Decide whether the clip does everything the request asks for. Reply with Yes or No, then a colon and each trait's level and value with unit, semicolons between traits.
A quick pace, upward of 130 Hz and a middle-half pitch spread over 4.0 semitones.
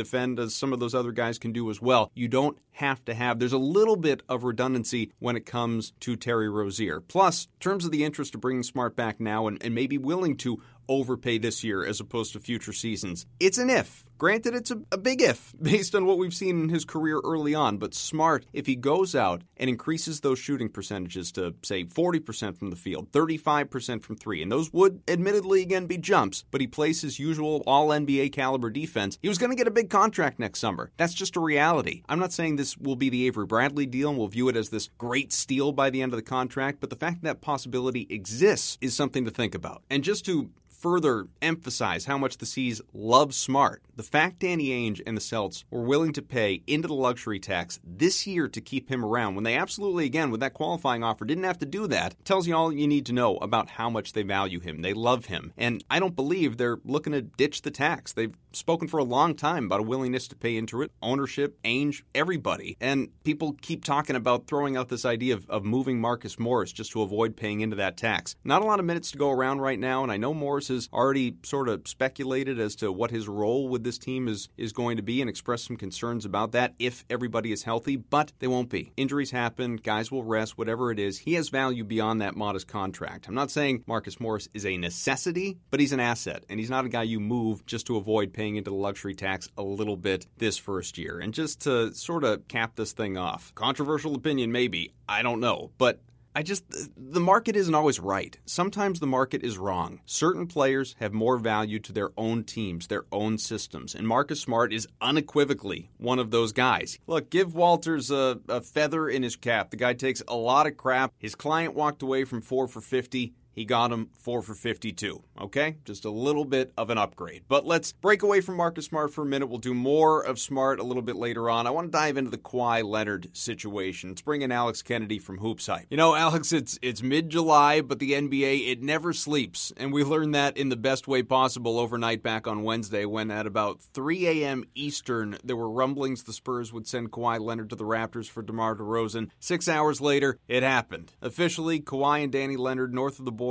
No: fast, 225 wpm; low, 125 Hz; average, 4.6 semitones